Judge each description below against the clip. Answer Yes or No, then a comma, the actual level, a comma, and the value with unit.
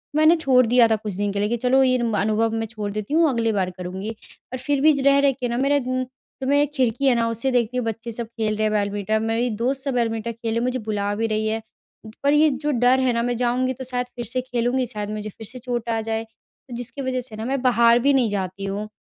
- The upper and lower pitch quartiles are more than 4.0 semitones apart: No, average, 2.9 semitones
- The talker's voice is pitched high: Yes, high, 235 Hz